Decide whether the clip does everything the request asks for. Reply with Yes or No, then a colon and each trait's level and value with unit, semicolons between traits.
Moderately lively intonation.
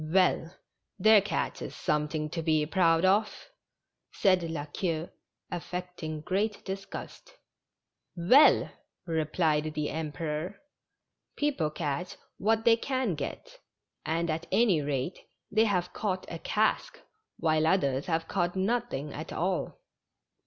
Yes: average, 4.1 semitones